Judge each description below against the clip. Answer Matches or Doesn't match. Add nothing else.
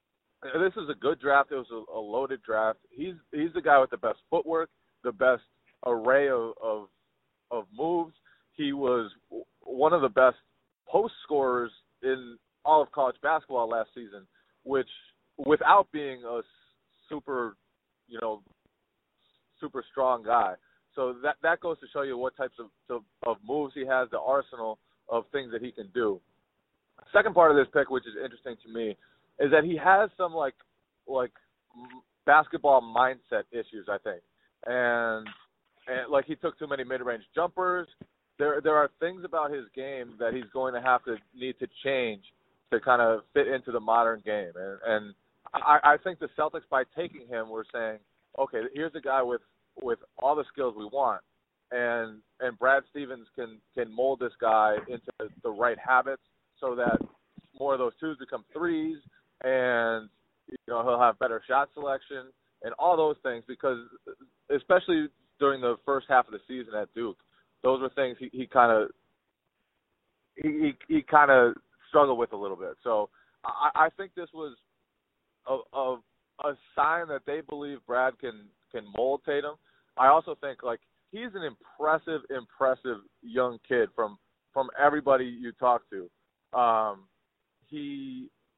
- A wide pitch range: Doesn't match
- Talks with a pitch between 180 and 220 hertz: Doesn't match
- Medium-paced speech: Matches